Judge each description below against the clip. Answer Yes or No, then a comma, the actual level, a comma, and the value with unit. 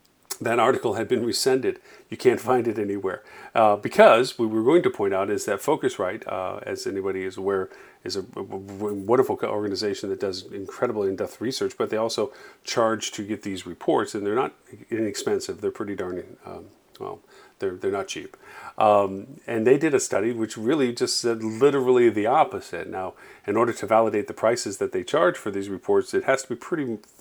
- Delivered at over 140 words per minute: Yes, average, 195 wpm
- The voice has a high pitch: No, medium, 140 Hz